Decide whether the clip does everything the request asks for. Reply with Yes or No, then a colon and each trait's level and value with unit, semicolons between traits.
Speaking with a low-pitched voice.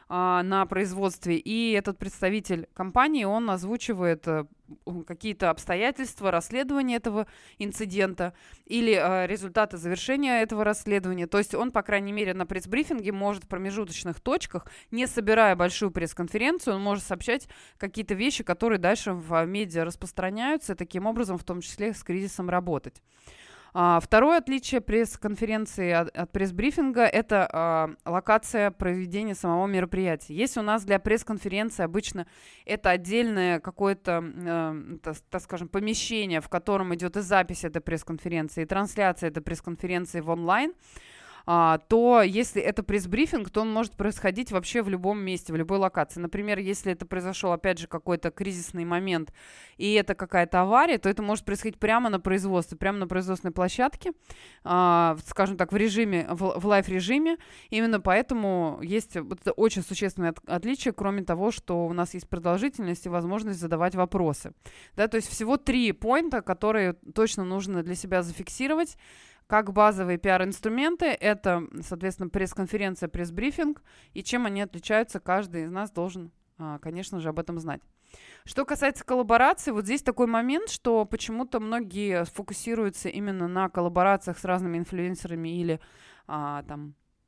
No: high, 195 Hz